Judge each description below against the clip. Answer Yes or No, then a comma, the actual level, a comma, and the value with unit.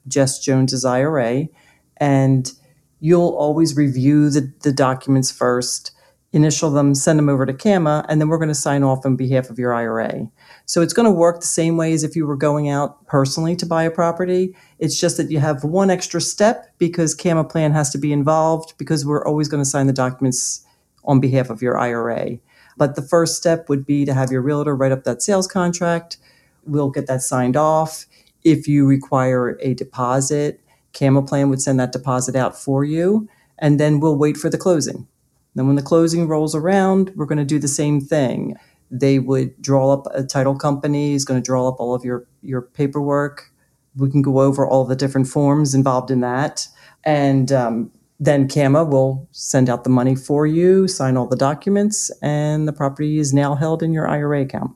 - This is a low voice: No, medium, 145 Hz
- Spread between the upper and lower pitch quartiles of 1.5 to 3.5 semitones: Yes, average, 2.9 semitones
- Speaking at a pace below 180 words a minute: No, fast, 205 wpm